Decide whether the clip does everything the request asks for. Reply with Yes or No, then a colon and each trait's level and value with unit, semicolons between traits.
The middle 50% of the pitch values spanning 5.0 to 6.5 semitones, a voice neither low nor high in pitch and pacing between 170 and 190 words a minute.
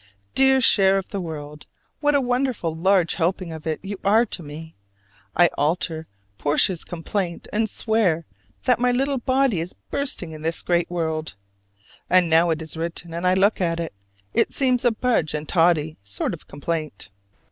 Yes: wide, 5.4 semitones; medium, 175 Hz; average, 175 wpm